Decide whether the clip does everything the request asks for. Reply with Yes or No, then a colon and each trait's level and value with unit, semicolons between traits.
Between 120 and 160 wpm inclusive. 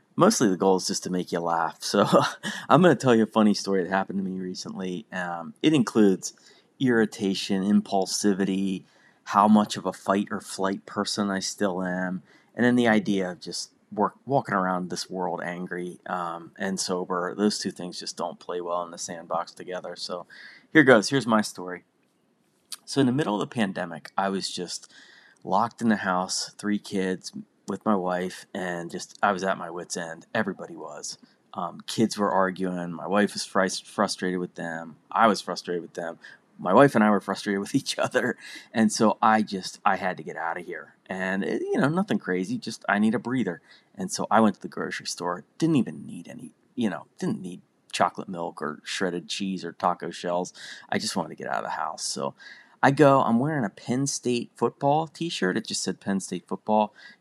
No: fast, 205 wpm